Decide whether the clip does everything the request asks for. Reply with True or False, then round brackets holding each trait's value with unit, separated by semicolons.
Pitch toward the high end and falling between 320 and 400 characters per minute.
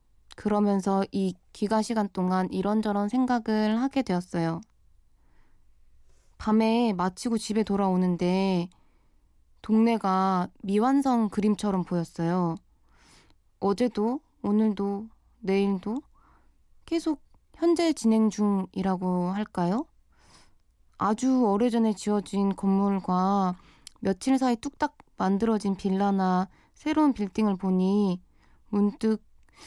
False (205 Hz; 215 characters per minute)